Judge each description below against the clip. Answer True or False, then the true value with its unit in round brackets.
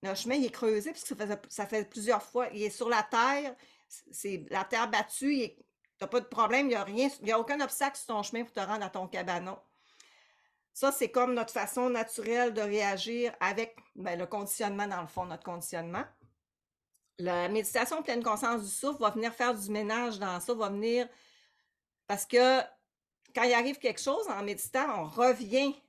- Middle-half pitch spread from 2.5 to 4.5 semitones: True (3.5 semitones)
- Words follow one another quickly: False (190 wpm)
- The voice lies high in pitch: True (230 Hz)